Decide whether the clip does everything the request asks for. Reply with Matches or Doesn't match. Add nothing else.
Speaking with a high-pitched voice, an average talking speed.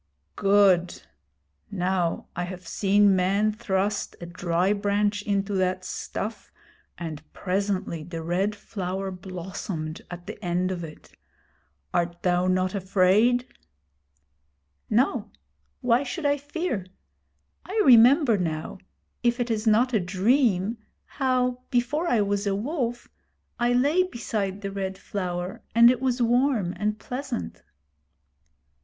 Doesn't match